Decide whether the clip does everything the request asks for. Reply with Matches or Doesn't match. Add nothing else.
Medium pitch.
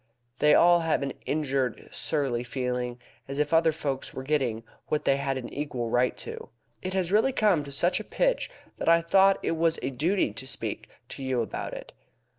Matches